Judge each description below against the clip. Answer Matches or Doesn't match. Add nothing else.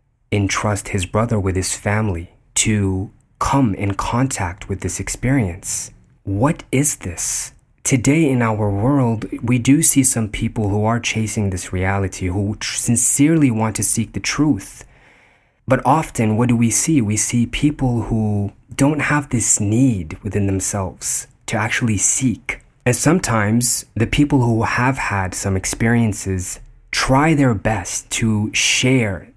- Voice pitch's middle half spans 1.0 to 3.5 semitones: Doesn't match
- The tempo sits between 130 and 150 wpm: Matches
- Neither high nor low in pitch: Doesn't match